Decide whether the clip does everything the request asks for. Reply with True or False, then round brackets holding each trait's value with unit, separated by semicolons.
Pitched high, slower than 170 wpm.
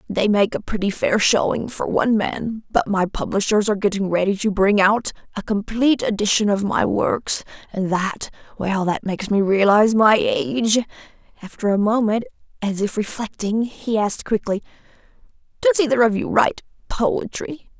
True (210 Hz; 160 wpm)